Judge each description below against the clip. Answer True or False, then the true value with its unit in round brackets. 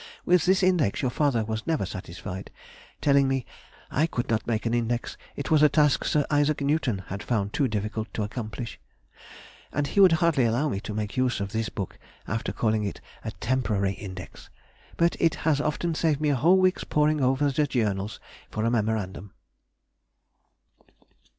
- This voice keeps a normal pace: True (175 wpm)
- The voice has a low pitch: True (125 Hz)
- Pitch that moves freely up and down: True (5.7 semitones)